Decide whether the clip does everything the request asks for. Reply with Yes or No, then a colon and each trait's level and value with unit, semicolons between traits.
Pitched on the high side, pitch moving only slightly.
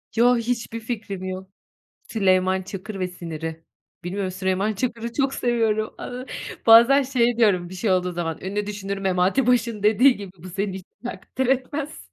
No: high, 205 Hz; average, 4.1 semitones